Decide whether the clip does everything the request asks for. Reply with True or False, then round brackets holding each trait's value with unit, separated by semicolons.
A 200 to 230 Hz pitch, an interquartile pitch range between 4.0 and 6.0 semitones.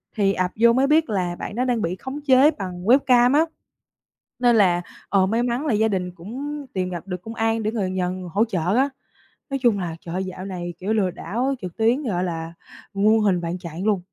True (205 Hz; 4.9 semitones)